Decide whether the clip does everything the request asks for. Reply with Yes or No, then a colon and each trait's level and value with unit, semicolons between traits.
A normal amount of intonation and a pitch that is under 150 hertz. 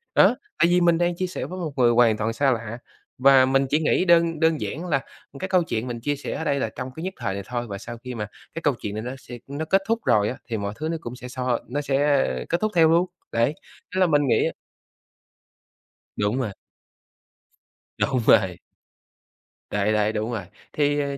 No: wide, 5.8 semitones; low, 135 Hz